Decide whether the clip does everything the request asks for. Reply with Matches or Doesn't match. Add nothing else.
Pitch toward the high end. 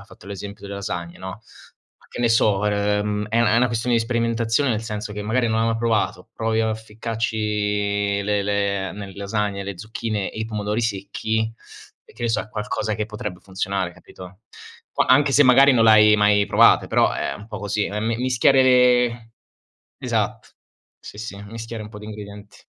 Doesn't match